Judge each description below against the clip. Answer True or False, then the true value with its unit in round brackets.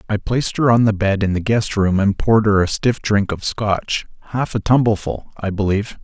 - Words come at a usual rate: False (220 wpm)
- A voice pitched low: True (105 Hz)